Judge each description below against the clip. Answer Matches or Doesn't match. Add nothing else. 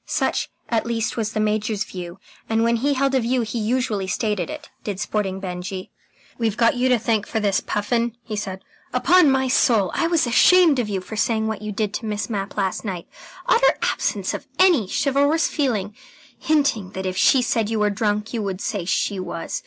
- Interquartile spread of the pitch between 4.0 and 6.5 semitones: Doesn't match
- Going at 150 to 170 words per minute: Doesn't match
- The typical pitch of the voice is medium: Doesn't match